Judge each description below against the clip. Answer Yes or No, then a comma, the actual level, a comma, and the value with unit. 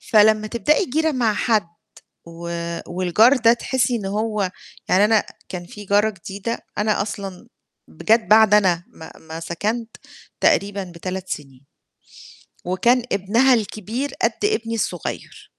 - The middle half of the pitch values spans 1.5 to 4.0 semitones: Yes, average, 3.6 semitones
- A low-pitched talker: No, high, 210 Hz